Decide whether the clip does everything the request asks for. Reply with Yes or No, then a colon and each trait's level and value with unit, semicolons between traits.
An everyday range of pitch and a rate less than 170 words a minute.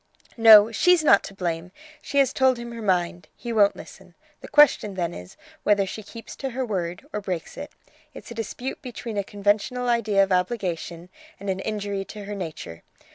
No: average, 4.1 semitones; average, 190 wpm